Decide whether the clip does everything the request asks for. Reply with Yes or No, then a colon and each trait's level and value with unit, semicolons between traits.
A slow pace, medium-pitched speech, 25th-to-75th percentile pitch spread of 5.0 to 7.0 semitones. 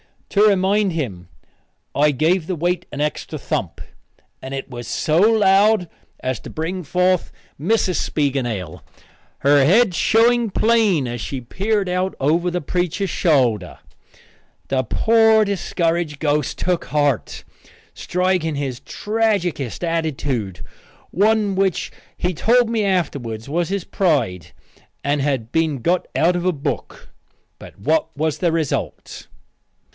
Yes: slow, 130 wpm; medium, 165 Hz; wide, 5.4 semitones